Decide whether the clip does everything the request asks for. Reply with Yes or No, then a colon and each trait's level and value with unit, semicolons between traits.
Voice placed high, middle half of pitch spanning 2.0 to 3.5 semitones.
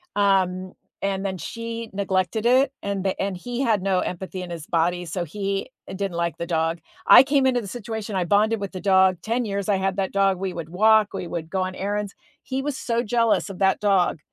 Yes: high, 195 Hz; average, 2.9 semitones